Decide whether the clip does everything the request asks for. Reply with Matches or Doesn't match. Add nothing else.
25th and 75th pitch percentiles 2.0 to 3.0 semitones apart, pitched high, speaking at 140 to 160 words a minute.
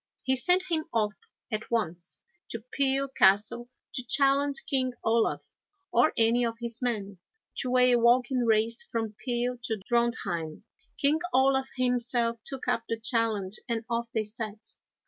Matches